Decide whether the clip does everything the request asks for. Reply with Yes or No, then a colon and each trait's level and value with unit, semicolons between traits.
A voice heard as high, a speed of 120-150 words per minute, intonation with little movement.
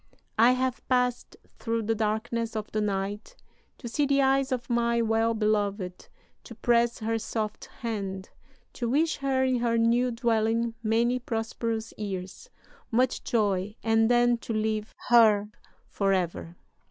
Yes: high, 230 Hz; average, 140 wpm; narrow, 2.0 semitones